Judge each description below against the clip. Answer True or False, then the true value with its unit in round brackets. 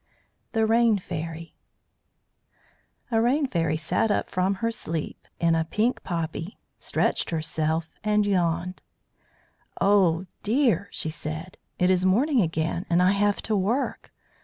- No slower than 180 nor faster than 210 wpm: False (135 wpm)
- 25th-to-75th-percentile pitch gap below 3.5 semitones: False (4.5 semitones)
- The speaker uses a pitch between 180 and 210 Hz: True (185 Hz)